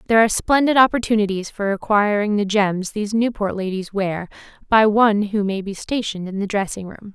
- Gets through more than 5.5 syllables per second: Yes, 5.8 syllables/s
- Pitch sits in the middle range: No, high, 205 Hz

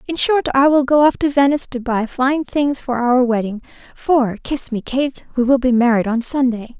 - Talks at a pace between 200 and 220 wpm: Yes, fast, 205 wpm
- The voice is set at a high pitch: Yes, very high, 260 Hz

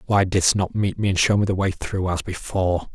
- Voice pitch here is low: Yes, very low, 95 Hz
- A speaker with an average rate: No, fast, 265 wpm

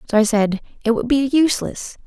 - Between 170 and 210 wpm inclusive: Yes, fast, 205 wpm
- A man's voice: No, female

